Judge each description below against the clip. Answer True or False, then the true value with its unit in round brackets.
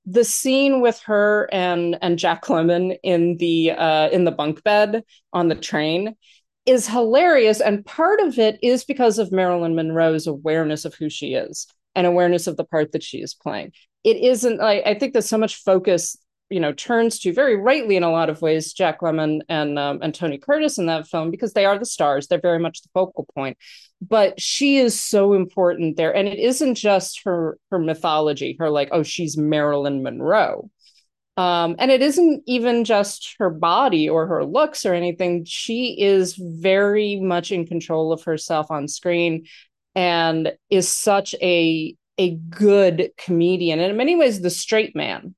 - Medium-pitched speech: True (180 Hz)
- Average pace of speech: True (190 wpm)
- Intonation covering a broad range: False (4.7 semitones)